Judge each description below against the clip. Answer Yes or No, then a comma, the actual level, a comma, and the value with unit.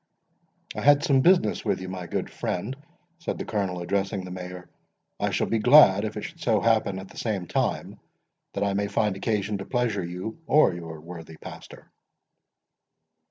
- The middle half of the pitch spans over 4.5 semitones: No, average, 3.7 semitones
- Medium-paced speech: Yes, average, 180 wpm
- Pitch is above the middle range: No, low, 100 Hz